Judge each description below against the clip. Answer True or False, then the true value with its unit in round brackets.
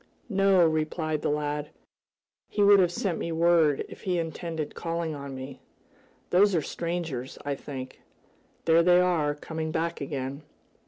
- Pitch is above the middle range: False (160 Hz)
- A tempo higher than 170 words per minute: False (150 wpm)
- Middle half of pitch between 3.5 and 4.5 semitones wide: False (2.9 semitones)